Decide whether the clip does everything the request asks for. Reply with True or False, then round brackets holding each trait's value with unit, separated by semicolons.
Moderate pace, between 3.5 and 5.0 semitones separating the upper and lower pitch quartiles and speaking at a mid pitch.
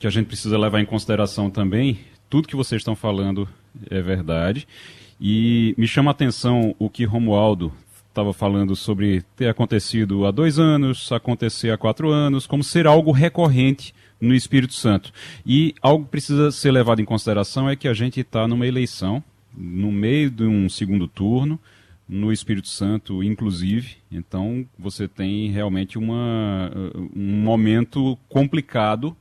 False (155 wpm; 4.1 semitones; 110 Hz)